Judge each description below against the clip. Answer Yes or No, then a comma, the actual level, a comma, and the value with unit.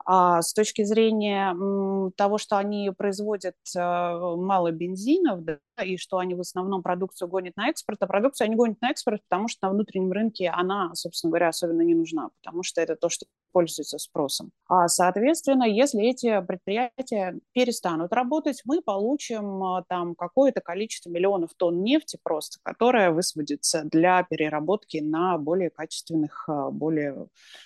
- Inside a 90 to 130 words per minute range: No, average, 150 wpm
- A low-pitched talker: No, high, 190 Hz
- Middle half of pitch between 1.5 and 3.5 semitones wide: No, average, 4.2 semitones